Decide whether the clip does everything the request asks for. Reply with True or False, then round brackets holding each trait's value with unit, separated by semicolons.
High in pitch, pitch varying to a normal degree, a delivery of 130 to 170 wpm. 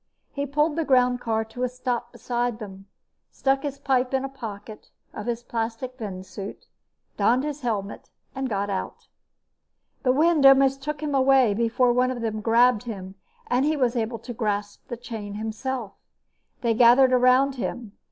True (245 Hz; 3.3 semitones; 165 wpm)